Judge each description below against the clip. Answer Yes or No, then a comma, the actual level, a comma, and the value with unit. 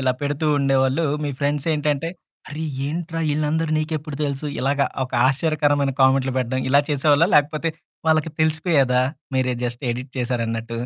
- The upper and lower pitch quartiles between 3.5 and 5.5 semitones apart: No, average, 2.8 semitones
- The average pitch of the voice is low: No, medium, 145 Hz